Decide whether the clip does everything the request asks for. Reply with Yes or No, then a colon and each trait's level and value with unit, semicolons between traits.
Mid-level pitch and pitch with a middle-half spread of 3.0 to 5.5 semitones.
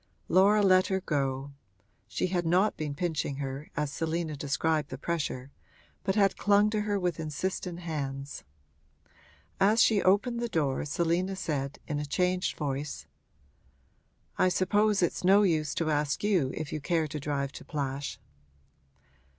Yes: medium, 165 Hz; average, 4.8 semitones